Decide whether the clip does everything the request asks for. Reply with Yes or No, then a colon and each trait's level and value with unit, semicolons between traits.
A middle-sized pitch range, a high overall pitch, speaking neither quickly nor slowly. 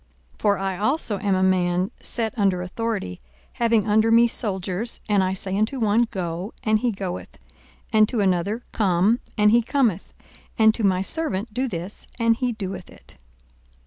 Yes: average, 3.4 semitones; high, 210 Hz; average, 175 wpm